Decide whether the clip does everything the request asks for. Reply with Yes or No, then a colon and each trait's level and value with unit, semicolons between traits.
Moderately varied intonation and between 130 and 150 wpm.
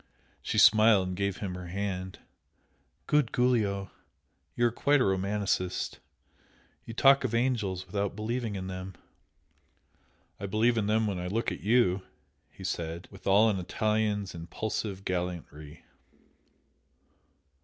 Yes: average, 3.2 semitones; slow, 135 wpm